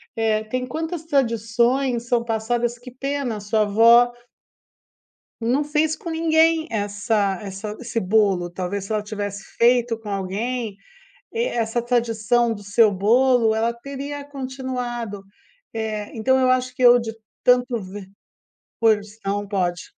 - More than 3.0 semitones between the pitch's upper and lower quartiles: Yes, average, 3.4 semitones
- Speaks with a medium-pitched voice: No, high, 230 Hz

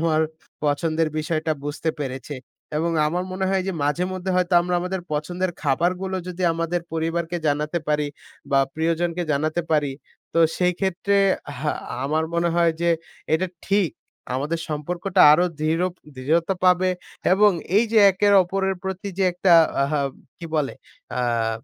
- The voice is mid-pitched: Yes, medium, 170 Hz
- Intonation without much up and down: No, average, 3.1 semitones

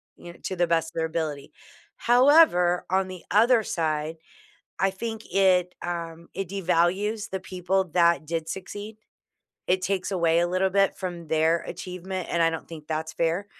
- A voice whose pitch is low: No, medium, 180 Hz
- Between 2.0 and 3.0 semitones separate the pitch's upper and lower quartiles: Yes, narrow, 2.6 semitones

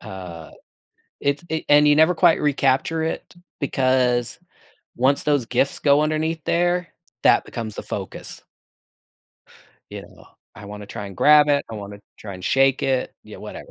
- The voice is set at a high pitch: No, low, 135 Hz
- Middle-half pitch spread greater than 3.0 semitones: Yes, average, 5.1 semitones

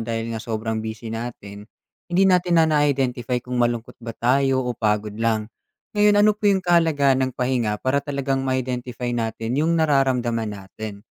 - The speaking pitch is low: Yes, low, 125 Hz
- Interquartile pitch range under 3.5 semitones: No, average, 4.0 semitones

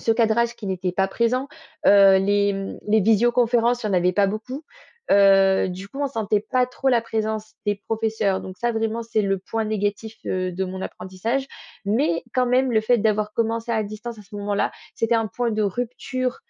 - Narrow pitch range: No, average, 3.0 semitones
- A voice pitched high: Yes, high, 220 Hz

